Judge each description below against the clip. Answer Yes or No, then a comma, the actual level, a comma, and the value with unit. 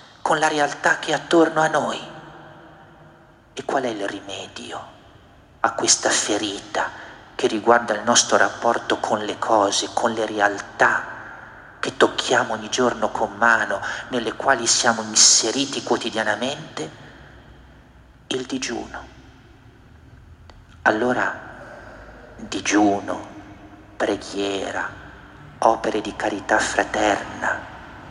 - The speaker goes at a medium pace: No, slow, 100 wpm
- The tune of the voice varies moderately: No, wide, 6.0 semitones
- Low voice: Yes, low, 120 Hz